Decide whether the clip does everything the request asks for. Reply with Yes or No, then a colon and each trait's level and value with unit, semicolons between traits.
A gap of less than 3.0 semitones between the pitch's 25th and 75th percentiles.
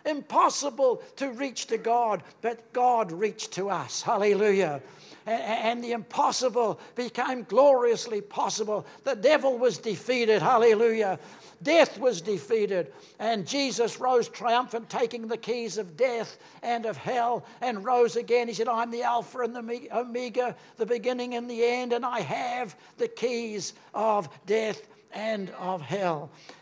Yes: narrow, 2.4 semitones